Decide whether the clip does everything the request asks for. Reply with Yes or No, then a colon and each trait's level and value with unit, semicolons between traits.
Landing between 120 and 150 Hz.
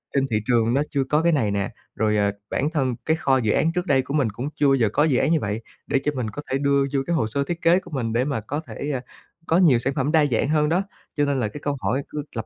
Yes: medium, 140 Hz